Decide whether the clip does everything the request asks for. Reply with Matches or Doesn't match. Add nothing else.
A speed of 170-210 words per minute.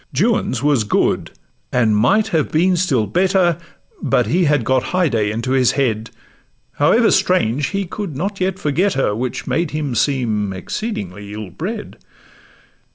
Doesn't match